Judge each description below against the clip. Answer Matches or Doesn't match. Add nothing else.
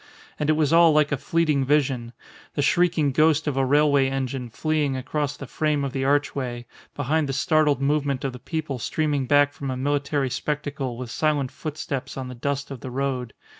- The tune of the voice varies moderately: Doesn't match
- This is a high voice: Doesn't match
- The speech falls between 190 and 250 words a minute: Matches